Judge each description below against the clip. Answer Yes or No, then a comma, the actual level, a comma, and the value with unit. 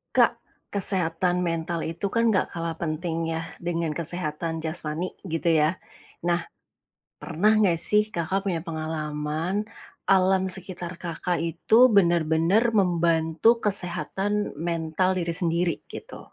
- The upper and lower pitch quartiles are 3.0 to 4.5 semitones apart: No, narrow, 2.5 semitones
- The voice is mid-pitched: Yes, medium, 170 Hz